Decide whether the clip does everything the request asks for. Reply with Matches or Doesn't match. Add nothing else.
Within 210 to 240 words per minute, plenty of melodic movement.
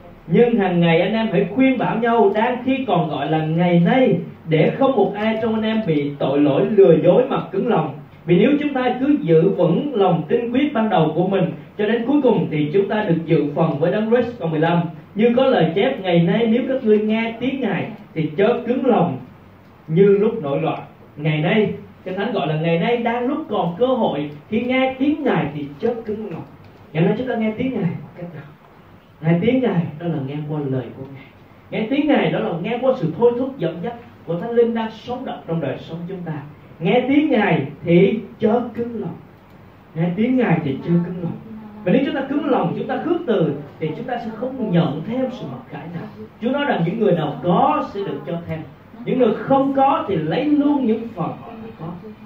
Matches